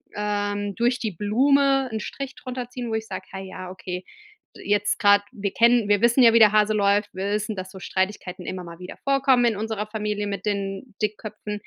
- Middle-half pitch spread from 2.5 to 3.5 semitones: Yes, average, 2.8 semitones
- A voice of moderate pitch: No, high, 210 Hz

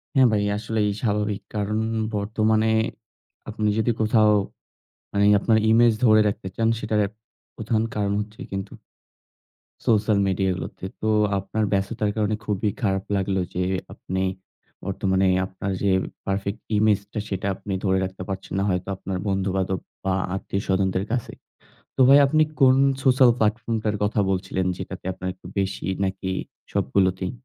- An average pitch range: No, narrow, 2.2 semitones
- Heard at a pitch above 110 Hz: No, low, 100 Hz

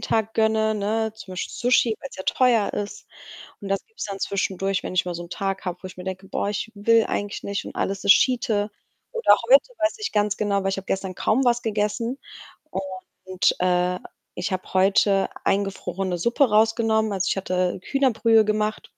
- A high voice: Yes, high, 205 Hz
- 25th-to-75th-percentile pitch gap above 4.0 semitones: No, average, 2.7 semitones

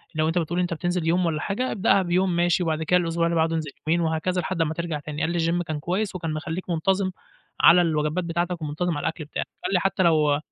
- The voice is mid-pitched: Yes, medium, 170 Hz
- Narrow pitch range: Yes, narrow, 2.2 semitones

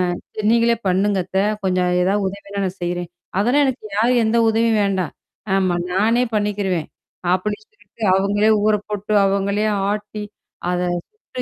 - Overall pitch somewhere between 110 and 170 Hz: No, high, 205 Hz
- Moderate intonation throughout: No, narrow, 2.3 semitones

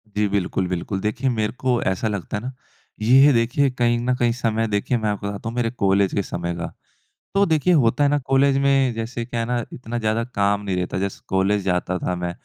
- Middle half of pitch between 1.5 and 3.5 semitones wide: No, average, 3.9 semitones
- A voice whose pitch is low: Yes, low, 115 Hz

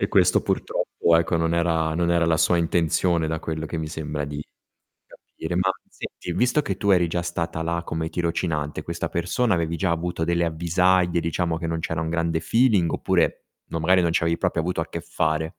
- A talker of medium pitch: No, very low, 85 Hz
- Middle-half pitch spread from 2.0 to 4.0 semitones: No, narrow, 1.3 semitones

